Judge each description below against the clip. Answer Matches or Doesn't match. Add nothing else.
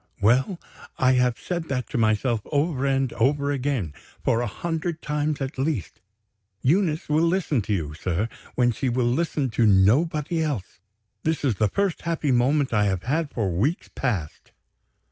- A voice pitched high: Doesn't match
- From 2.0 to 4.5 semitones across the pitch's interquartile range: Doesn't match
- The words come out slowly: Doesn't match